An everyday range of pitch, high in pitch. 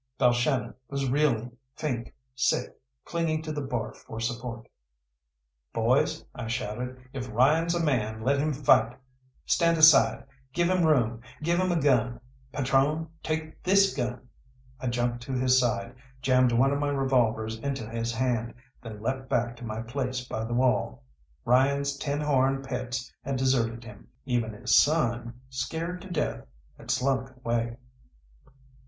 No: average, 3.2 semitones; low, 130 Hz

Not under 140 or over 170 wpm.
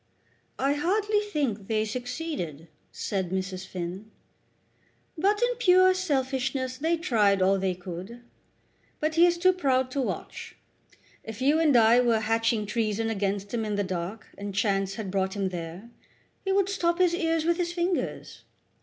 Yes: average, 160 wpm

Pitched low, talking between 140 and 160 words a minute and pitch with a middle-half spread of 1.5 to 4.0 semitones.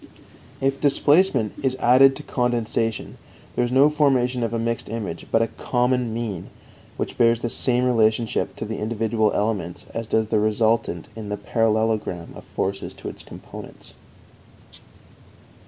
Yes: low, 115 Hz; average, 150 wpm; narrow, 2.4 semitones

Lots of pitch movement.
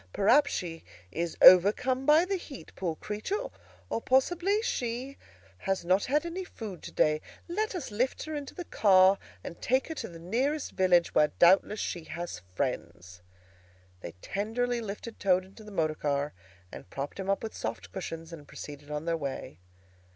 Yes: wide, 7.9 semitones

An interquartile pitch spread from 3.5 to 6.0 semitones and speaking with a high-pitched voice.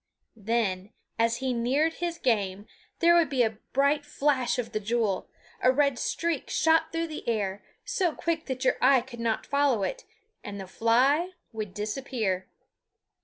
Yes: average, 5.2 semitones; very high, 255 Hz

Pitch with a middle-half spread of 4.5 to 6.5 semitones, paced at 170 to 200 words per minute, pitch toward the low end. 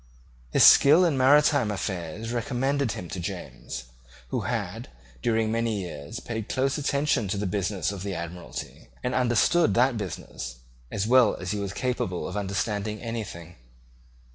No: average, 4.9 semitones; average, 150 wpm; low, 110 Hz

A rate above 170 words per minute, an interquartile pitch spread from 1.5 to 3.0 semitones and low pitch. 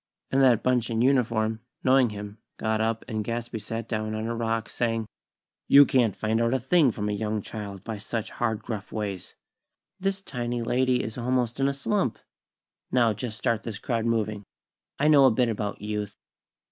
Yes: average, 185 wpm; narrow, 2.5 semitones; low, 115 Hz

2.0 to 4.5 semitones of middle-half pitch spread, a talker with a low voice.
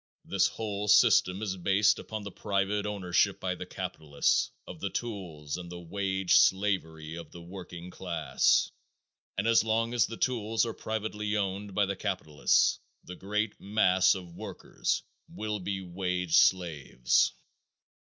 Yes: average, 3.0 semitones; very low, 95 Hz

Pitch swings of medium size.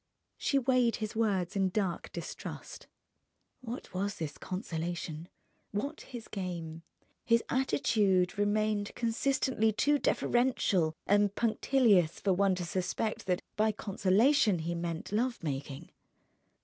Yes: average, 4.5 semitones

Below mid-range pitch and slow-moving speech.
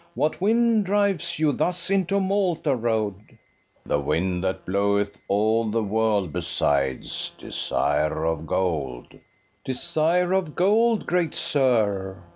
Yes: low, 115 Hz; slow, 125 wpm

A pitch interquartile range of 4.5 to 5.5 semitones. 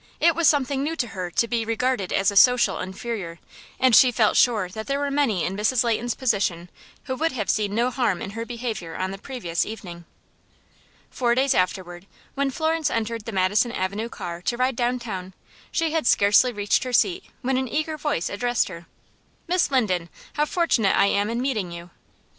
Yes: average, 5.1 semitones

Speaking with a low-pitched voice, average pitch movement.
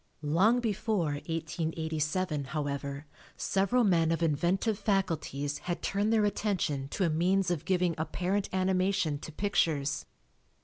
No: medium, 175 Hz; average, 4.2 semitones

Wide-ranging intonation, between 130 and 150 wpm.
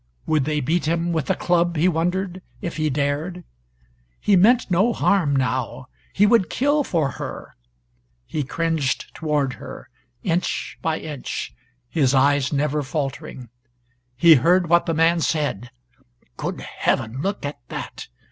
No: average, 3.7 semitones; average, 145 wpm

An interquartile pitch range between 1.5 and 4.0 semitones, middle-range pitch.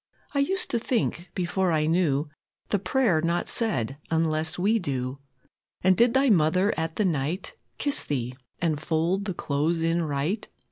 No: average, 4.4 semitones; medium, 170 Hz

